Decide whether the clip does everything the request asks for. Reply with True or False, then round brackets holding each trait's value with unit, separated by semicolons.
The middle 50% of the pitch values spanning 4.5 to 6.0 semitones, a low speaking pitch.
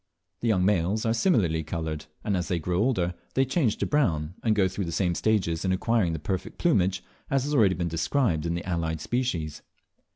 True (5.2 semitones; 95 Hz)